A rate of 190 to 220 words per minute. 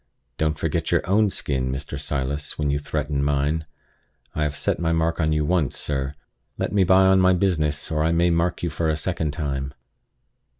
Yes: average, 200 wpm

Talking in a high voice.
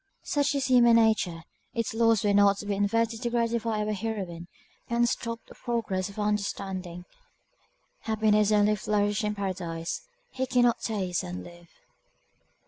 Yes: high, 210 Hz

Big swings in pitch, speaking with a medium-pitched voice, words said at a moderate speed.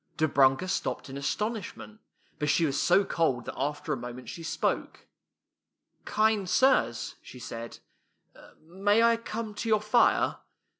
Yes: wide, 7.8 semitones; medium, 170 Hz; average, 150 wpm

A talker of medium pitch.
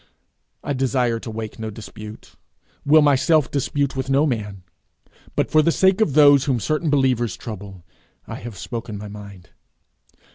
No: low, 125 Hz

